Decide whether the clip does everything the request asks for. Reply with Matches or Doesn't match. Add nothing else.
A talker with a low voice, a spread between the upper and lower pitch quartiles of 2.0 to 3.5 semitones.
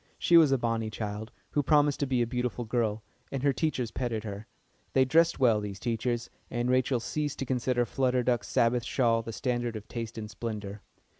Matches